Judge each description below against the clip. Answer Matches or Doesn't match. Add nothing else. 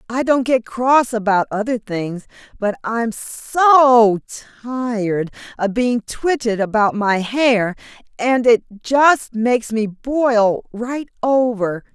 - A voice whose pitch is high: Matches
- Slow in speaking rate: Matches